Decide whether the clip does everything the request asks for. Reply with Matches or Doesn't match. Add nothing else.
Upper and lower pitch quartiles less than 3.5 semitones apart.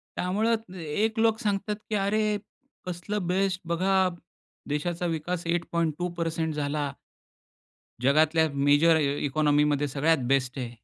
Doesn't match